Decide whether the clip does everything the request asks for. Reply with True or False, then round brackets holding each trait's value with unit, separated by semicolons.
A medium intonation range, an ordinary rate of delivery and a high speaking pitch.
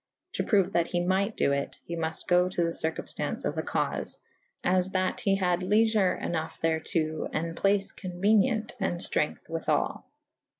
False (3.0 semitones; 175 wpm; 180 Hz)